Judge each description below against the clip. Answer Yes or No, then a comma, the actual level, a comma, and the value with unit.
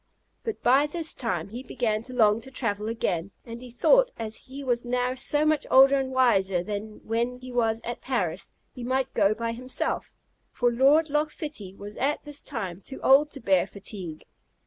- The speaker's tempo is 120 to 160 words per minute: No, average, 190 wpm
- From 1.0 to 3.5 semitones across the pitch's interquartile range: No, average, 4.0 semitones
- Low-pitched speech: No, high, 245 Hz